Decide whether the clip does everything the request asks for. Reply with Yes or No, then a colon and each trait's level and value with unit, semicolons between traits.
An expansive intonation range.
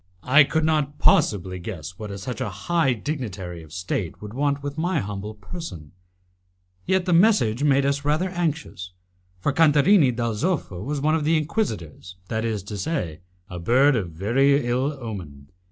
Yes: wide, 7.7 semitones